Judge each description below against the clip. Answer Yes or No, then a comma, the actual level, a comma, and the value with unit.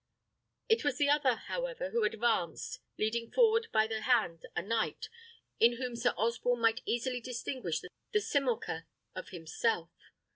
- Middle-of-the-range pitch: No, high, 235 Hz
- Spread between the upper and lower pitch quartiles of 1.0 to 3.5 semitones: Yes, average, 3.1 semitones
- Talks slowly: No, average, 145 wpm